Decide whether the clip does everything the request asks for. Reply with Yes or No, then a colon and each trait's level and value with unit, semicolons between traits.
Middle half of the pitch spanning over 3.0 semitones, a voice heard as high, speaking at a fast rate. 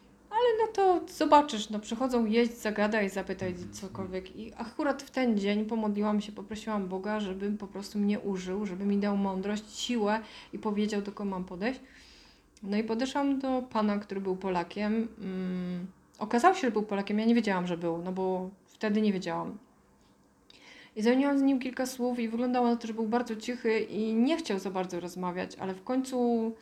Yes: average, 3.7 semitones; high, 215 Hz; fast, 185 wpm